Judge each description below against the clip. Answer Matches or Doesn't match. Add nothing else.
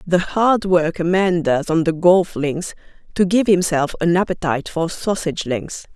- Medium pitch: Matches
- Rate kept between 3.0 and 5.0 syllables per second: Matches